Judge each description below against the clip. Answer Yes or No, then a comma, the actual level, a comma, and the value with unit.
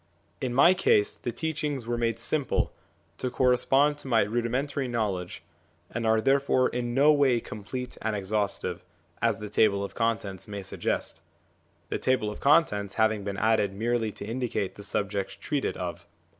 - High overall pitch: No, low, 115 Hz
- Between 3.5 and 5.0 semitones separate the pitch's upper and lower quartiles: Yes, average, 4.0 semitones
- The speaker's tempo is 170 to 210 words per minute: No, average, 160 wpm